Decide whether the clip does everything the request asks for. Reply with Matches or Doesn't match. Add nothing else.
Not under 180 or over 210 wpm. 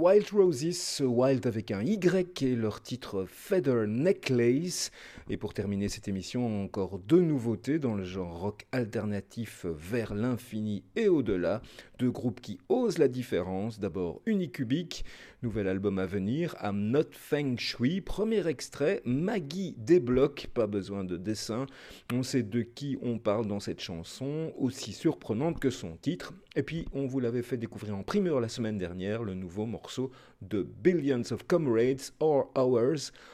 Doesn't match